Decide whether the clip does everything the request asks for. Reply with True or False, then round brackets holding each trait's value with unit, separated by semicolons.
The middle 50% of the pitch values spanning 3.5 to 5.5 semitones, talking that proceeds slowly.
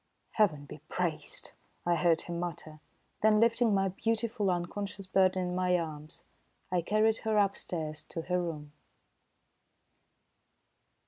True (3.8 semitones; 125 wpm)